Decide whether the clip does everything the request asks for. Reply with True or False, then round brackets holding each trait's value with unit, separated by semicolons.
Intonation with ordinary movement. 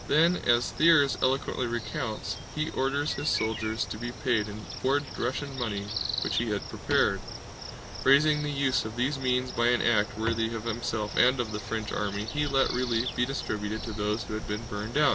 True (3.9 semitones)